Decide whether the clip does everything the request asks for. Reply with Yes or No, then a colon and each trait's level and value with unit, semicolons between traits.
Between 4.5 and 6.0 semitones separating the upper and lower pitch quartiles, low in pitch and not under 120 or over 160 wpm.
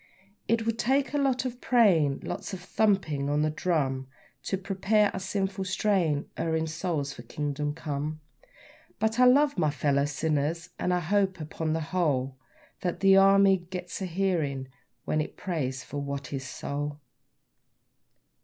No: average, 5.0 semitones; medium, 165 Hz; average, 155 wpm